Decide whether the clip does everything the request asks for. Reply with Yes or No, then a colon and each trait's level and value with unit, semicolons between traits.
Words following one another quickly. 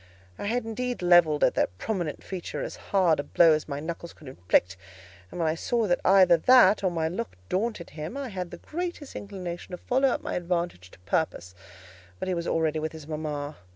Yes: fast, 210 wpm